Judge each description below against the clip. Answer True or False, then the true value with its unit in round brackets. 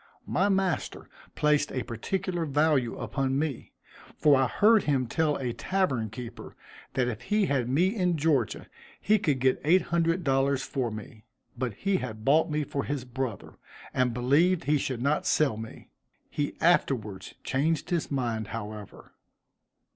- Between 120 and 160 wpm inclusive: True (155 wpm)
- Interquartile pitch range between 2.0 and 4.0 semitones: False (4.9 semitones)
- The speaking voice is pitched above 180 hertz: False (140 Hz)